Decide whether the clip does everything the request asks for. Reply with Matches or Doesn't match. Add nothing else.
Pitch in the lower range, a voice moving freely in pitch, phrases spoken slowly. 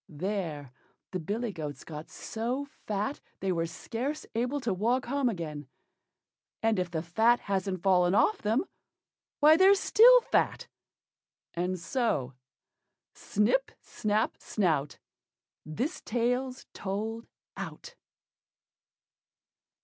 Doesn't match